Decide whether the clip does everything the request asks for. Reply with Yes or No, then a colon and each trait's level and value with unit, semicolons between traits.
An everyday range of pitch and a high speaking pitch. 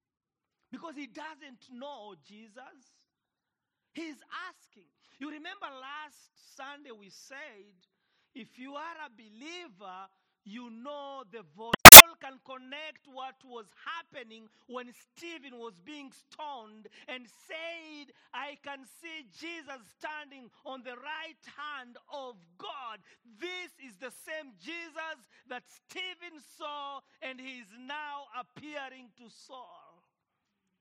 Yes: average, 4.1 semitones; very high, 275 Hz